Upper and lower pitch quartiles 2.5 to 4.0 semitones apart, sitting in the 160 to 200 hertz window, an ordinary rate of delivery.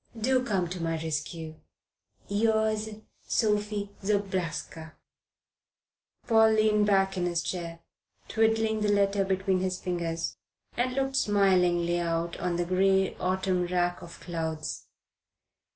No: average, 3.4 semitones; high, 190 Hz; slow, 120 wpm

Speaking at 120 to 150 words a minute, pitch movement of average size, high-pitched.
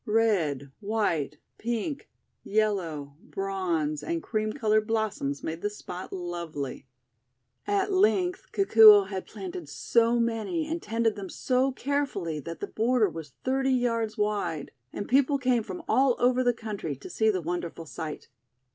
No: average, 145 wpm; wide, 6.4 semitones; high, 215 Hz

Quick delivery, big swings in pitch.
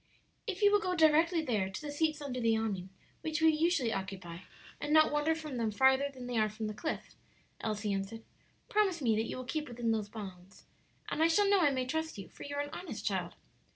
Yes: fast, 230 wpm; wide, 6.6 semitones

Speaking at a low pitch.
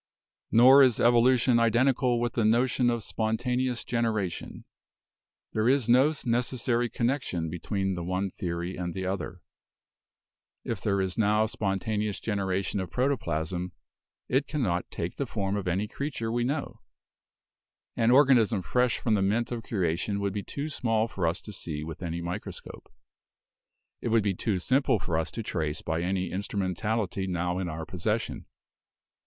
Yes: low, 105 Hz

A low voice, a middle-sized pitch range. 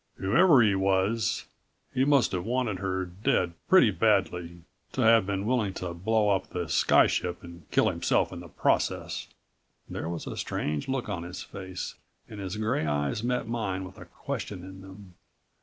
Yes: very low, 95 Hz; average, 3.8 semitones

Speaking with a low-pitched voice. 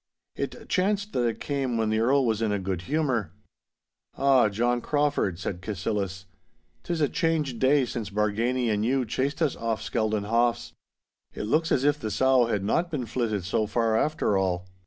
Yes: low, 120 Hz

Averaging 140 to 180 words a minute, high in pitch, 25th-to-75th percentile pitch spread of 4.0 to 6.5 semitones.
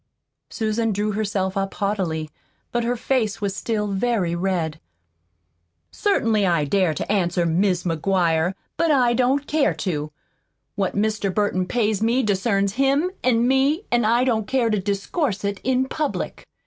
Yes: average, 150 wpm; high, 210 Hz; average, 4.4 semitones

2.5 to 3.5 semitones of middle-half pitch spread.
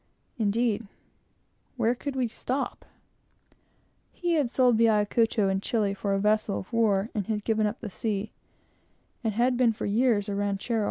Yes: average, 2.8 semitones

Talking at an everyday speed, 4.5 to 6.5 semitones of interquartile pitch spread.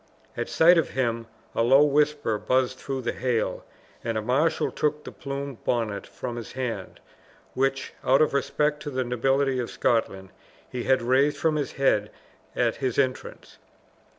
No: average, 165 wpm; average, 2.9 semitones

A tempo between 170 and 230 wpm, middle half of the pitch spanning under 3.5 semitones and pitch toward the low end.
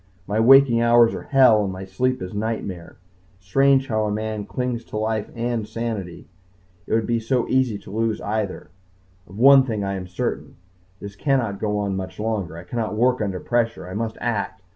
Yes: average, 190 wpm; average, 3.0 semitones; low, 110 Hz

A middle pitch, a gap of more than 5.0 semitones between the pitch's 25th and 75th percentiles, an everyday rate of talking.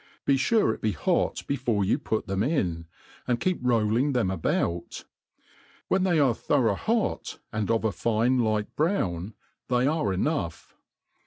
No: low, 115 Hz; wide, 5.6 semitones; average, 155 wpm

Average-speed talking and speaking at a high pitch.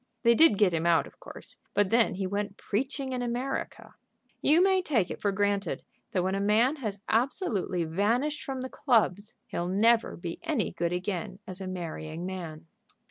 Yes: average, 185 wpm; high, 205 Hz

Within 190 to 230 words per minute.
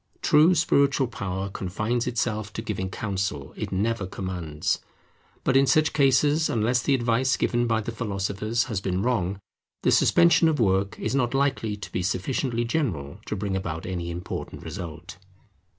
No: average, 160 wpm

